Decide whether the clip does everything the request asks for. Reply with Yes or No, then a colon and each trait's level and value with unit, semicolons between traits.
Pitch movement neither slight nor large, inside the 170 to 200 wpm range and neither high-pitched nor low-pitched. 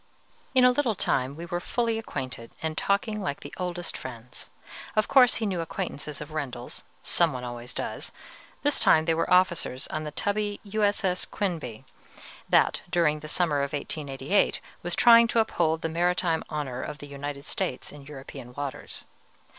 No: wide, 6.0 semitones; average, 175 wpm; medium, 160 Hz